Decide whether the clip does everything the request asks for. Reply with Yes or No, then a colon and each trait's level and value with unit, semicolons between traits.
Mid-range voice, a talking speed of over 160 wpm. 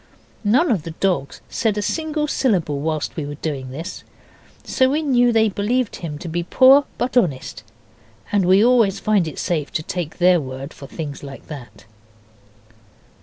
Yes: medium, 180 Hz; average, 170 wpm